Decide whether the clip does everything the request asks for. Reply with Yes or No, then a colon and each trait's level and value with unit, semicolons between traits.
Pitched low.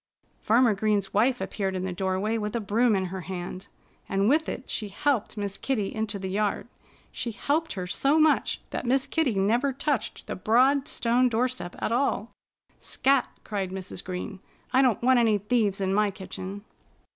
No: high, 215 Hz